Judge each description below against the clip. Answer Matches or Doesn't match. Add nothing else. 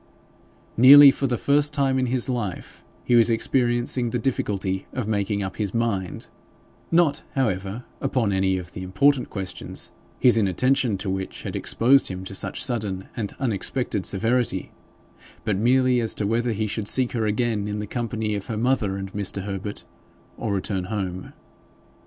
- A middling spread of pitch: Matches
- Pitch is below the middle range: Matches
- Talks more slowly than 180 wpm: Matches